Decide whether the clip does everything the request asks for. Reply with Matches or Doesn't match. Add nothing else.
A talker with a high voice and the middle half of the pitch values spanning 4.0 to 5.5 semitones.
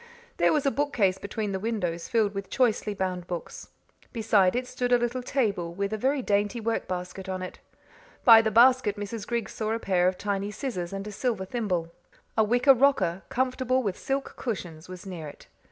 Matches